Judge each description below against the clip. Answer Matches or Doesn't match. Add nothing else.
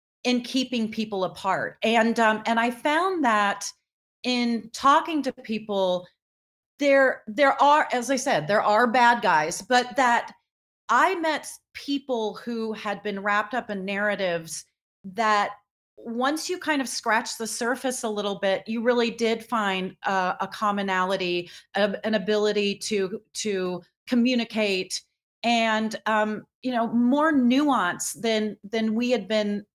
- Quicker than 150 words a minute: Doesn't match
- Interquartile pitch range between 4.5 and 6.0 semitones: Doesn't match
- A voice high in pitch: Matches